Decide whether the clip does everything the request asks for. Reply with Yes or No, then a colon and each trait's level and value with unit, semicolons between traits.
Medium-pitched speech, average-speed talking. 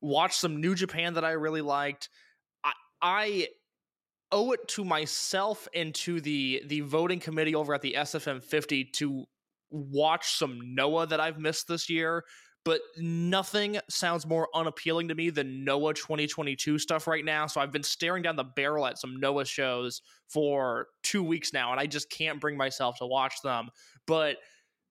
Yes: medium, 155 Hz; average, 170 wpm